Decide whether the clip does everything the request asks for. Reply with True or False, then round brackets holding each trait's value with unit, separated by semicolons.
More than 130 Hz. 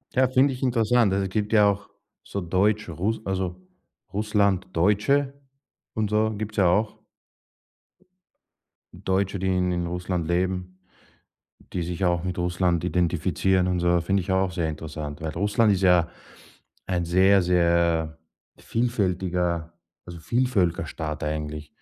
False (90 Hz)